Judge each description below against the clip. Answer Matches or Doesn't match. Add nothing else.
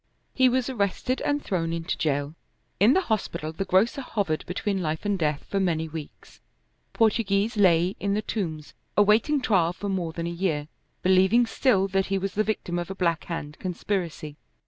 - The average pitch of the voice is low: Doesn't match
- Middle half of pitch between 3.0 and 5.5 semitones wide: Matches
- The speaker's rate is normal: Matches